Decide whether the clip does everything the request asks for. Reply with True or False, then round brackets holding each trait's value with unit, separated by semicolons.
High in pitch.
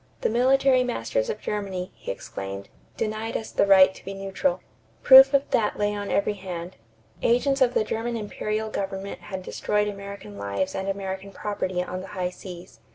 True (200 Hz)